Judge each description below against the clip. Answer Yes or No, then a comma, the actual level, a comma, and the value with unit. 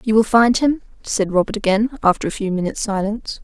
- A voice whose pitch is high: Yes, high, 210 Hz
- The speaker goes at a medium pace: No, fast, 210 wpm